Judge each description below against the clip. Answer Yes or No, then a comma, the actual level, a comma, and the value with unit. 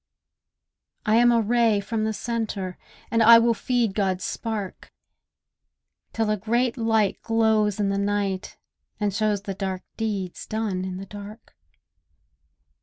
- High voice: Yes, high, 215 Hz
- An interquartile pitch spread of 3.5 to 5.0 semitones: No, narrow, 2.4 semitones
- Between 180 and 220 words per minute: No, average, 140 wpm